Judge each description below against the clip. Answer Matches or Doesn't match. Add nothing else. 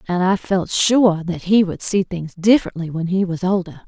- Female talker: Matches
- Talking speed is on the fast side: Matches